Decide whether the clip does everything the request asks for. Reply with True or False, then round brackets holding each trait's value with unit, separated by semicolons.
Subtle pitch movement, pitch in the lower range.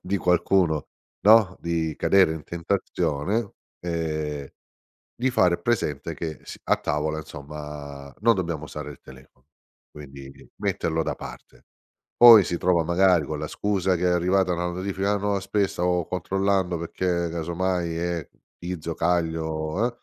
False (3.4 semitones; 85 Hz)